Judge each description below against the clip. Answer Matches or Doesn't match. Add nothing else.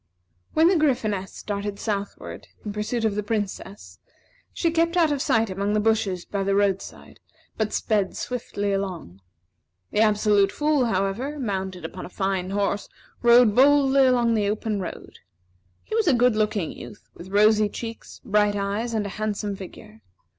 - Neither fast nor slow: Matches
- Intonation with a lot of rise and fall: Doesn't match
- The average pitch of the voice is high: Matches